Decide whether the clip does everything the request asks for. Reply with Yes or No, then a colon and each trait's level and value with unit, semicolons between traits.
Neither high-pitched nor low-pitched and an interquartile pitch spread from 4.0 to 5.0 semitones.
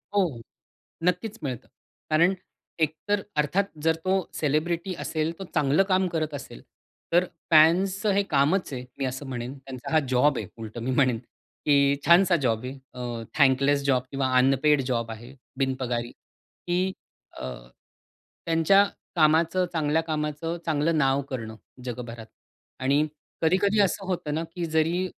Yes: medium, 150 Hz; average, 4.7 semitones